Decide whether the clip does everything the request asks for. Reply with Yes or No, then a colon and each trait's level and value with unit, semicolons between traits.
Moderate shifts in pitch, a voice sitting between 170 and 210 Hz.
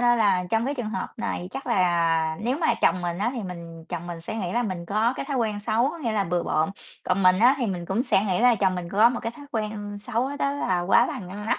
Yes: average, 4.8 semitones; high, 205 Hz